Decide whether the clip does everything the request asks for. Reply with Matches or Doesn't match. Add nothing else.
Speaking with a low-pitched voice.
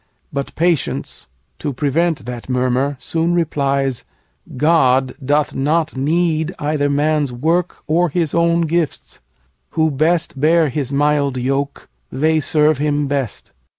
Doesn't match